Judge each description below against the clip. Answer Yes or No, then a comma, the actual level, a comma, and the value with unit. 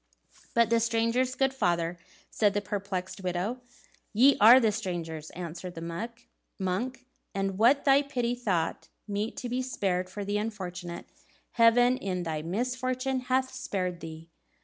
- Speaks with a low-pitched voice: No, high, 210 Hz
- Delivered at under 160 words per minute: Yes, average, 150 wpm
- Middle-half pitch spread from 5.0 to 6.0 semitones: Yes, wide, 5.5 semitones